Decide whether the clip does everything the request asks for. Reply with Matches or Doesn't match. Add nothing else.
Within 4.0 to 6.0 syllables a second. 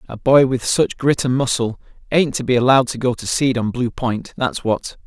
Matches